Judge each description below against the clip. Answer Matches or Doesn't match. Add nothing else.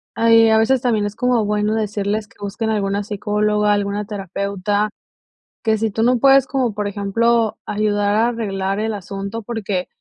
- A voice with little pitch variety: Matches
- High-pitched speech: Matches